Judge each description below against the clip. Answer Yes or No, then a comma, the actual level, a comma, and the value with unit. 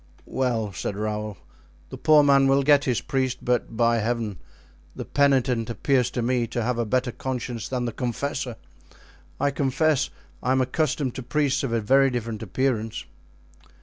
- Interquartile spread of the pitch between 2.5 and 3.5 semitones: Yes, average, 2.8 semitones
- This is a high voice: No, low, 125 Hz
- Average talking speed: Yes, average, 165 wpm